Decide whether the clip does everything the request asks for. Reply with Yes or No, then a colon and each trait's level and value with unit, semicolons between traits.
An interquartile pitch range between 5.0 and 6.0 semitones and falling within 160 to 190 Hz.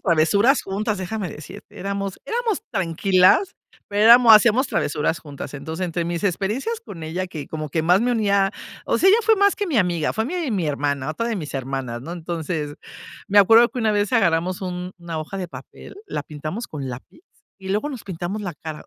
Yes: wide, 5.6 semitones; medium, 185 Hz